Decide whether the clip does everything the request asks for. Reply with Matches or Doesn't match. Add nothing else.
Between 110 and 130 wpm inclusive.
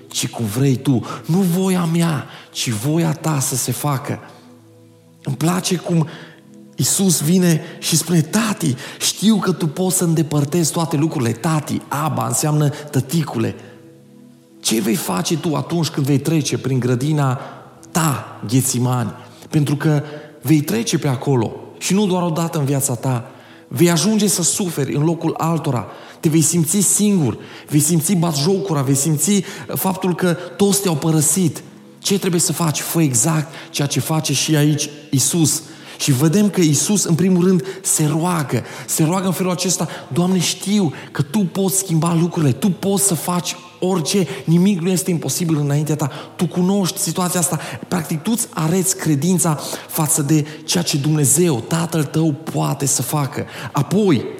Doesn't match